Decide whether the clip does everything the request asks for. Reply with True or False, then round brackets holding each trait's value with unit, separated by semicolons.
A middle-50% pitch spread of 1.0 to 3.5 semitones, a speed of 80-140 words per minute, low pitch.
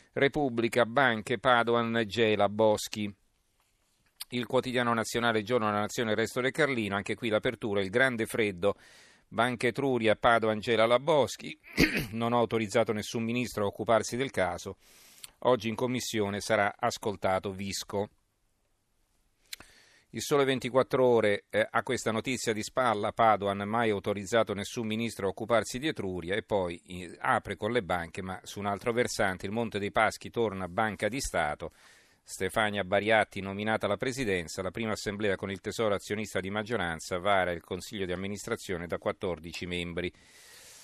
False (2.8 semitones; 150 wpm; 110 Hz)